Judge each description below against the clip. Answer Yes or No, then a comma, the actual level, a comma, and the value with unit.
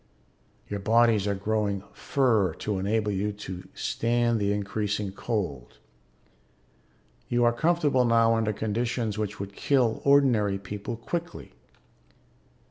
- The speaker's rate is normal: No, slow, 120 wpm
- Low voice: Yes, low, 110 Hz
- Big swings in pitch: No, average, 2.8 semitones